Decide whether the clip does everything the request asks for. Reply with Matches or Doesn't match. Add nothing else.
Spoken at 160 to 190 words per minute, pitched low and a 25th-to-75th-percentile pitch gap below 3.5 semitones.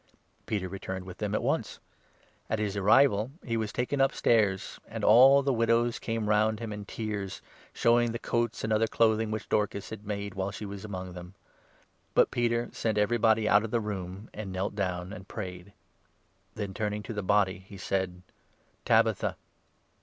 Matches